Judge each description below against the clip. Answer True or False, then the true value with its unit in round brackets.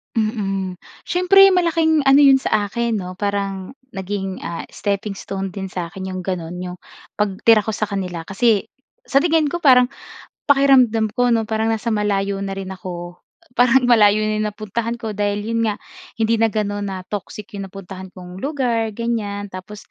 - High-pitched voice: True (210 Hz)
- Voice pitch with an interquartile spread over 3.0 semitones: True (3.4 semitones)